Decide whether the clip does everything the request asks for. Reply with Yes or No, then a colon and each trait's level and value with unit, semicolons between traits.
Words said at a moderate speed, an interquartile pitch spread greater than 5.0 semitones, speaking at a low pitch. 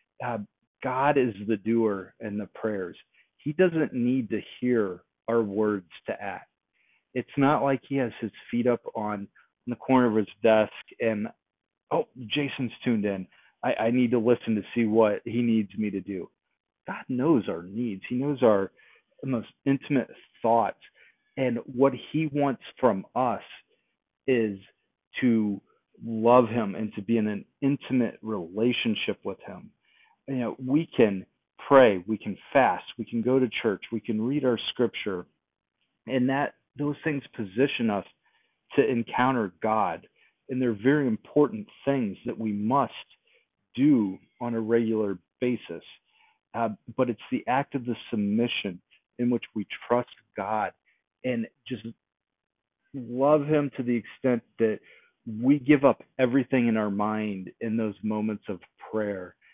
No: average, 155 wpm; average, 3.7 semitones; low, 120 Hz